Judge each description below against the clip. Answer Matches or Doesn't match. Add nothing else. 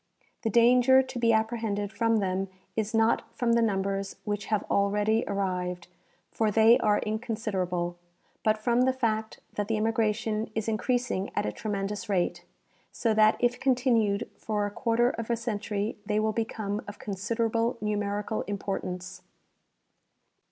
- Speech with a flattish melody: Matches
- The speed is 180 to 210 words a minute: Doesn't match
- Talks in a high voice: Matches